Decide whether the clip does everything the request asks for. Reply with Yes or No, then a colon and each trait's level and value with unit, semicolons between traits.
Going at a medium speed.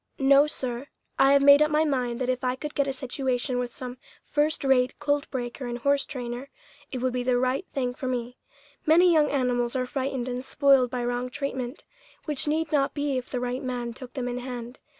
No: fast, 215 wpm